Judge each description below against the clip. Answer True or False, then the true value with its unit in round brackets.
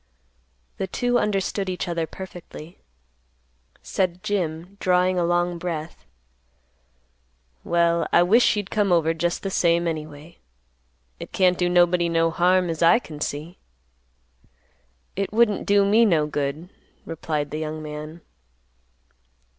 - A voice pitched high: False (175 Hz)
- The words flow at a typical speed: False (130 wpm)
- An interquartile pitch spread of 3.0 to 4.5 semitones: False (2.6 semitones)